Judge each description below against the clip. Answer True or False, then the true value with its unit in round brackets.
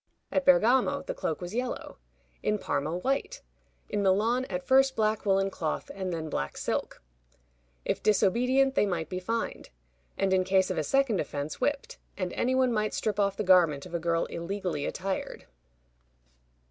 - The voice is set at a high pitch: True (195 Hz)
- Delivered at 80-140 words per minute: False (170 wpm)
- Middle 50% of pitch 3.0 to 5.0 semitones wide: False (5.4 semitones)